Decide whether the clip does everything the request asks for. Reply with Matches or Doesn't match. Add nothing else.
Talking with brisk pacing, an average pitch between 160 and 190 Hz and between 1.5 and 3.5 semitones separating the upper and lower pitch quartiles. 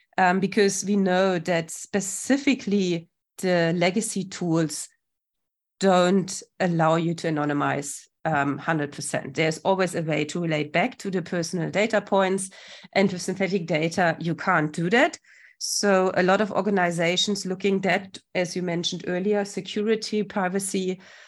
Doesn't match